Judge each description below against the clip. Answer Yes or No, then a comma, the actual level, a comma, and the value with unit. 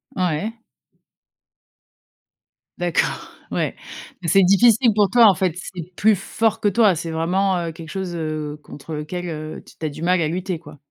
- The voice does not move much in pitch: No, average, 3.6 semitones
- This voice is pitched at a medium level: Yes, medium, 180 Hz